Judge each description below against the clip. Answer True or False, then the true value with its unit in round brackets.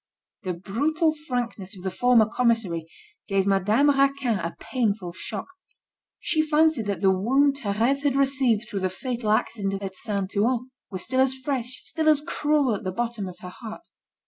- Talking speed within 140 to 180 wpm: True (170 wpm)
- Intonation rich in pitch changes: True (5.8 semitones)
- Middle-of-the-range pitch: False (230 Hz)